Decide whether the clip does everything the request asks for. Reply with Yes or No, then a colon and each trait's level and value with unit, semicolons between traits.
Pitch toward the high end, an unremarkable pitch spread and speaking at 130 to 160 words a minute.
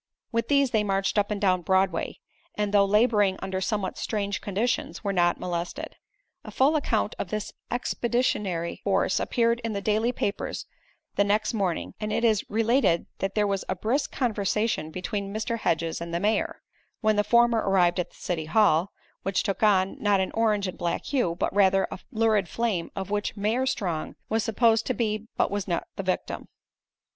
No: high, 205 Hz; average, 3.0 semitones; average, 185 wpm